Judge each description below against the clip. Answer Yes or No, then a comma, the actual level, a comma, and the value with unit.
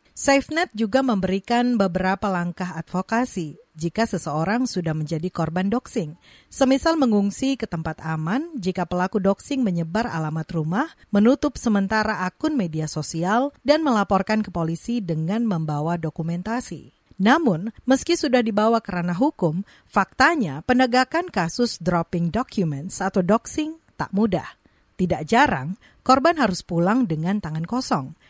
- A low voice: No, high, 200 Hz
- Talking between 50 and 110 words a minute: No, average, 125 wpm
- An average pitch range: No, wide, 6.2 semitones